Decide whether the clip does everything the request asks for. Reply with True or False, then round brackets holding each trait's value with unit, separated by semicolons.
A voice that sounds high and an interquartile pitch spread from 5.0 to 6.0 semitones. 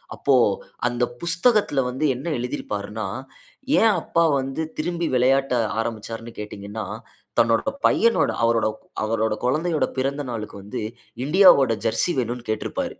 False (125 Hz; 5.4 semitones)